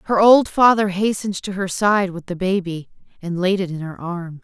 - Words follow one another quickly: Yes, fast, 215 wpm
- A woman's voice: Yes, female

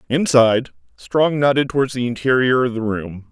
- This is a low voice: Yes, low, 125 Hz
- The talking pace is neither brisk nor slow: Yes, average, 165 wpm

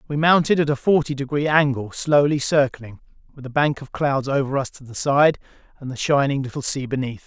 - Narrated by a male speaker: Yes, male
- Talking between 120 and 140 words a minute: No, fast, 205 wpm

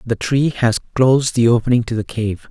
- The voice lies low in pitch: Yes, low, 120 Hz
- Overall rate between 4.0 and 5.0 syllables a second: No, 5.3 syllables/s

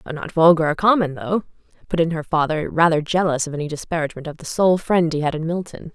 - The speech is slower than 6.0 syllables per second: No, 6.1 syllables/s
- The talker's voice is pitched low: No, medium, 165 Hz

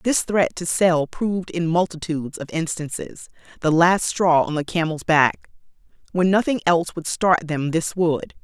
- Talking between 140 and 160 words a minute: No, average, 170 wpm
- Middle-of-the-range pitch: Yes, medium, 170 Hz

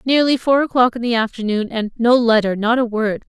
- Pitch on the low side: No, high, 235 Hz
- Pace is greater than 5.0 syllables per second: Yes, 5.5 syllables/s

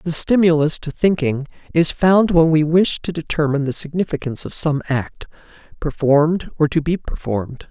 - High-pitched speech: No, medium, 155 Hz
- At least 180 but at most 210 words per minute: No, average, 165 wpm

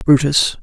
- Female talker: No, male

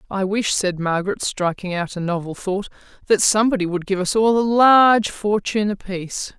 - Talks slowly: No, average, 180 wpm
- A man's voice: No, female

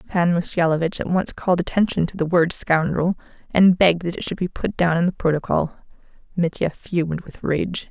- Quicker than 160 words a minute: Yes, average, 190 wpm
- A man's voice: No, female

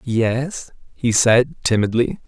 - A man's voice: Yes, male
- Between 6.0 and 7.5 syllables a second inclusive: No, 3.3 syllables/s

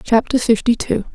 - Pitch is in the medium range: No, high, 230 Hz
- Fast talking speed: No, average, 155 wpm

